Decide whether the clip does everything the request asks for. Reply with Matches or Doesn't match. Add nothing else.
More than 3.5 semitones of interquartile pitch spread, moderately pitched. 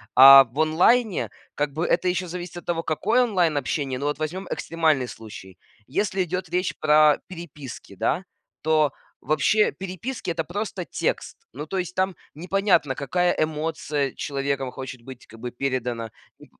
Matches